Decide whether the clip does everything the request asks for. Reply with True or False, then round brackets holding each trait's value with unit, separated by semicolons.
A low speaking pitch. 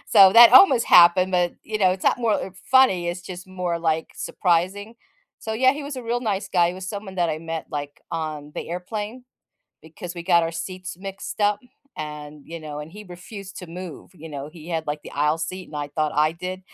False (180 Hz)